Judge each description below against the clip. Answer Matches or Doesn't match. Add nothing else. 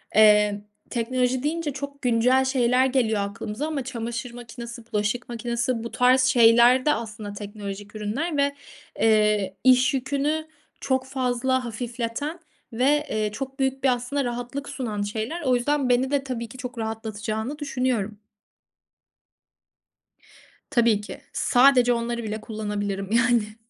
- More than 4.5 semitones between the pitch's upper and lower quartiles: Doesn't match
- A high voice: Matches